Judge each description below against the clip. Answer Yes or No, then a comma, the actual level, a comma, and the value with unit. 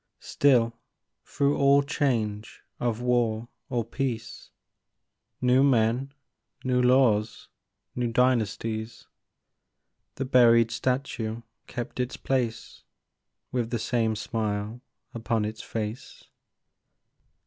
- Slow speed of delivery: Yes, slow, 95 wpm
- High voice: No, low, 120 Hz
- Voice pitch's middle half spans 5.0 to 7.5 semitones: No, narrow, 2.4 semitones